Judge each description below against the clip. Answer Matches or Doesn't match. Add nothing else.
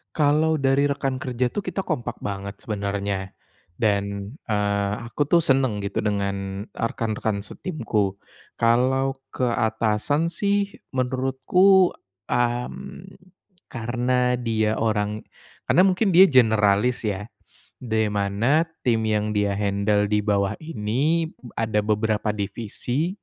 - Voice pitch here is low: Matches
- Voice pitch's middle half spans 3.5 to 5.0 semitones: Matches